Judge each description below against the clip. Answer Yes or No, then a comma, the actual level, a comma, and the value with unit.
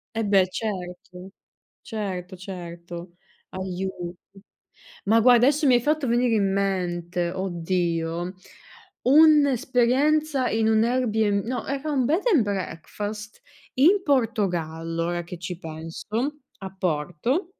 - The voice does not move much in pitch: No, wide, 6.0 semitones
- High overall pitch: Yes, high, 200 Hz